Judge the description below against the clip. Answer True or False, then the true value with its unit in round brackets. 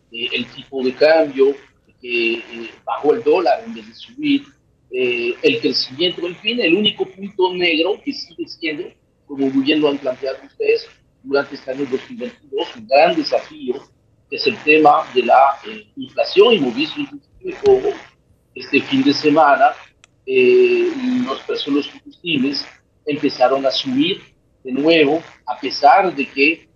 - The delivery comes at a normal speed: True (150 wpm)